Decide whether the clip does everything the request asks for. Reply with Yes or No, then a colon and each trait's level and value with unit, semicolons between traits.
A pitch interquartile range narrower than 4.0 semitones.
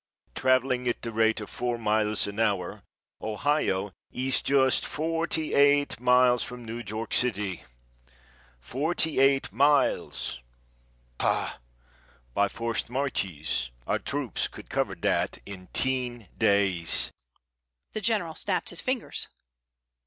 No: average, 5.0 semitones